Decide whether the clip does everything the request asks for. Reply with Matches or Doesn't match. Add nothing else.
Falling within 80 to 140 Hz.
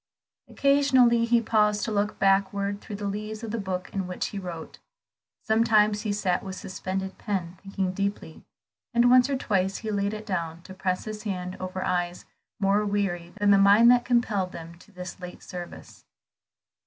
Doesn't match